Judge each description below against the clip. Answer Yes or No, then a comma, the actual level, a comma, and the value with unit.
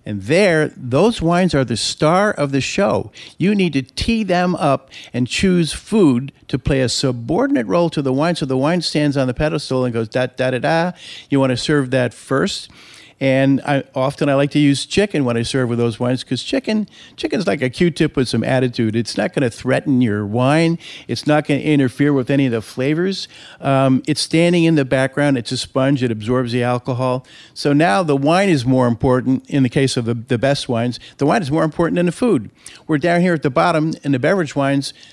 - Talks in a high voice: No, medium, 140 Hz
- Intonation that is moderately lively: Yes, average, 3.8 semitones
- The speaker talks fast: Yes, fast, 225 wpm